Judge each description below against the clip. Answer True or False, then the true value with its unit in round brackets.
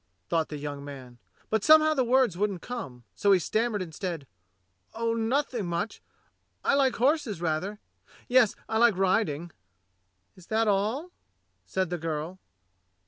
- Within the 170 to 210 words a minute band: False (140 wpm)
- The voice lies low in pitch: False (200 Hz)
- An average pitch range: False (6.1 semitones)